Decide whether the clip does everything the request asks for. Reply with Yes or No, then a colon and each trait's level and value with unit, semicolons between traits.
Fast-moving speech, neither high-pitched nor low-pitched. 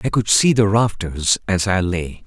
No: fast, 210 wpm; low, 100 Hz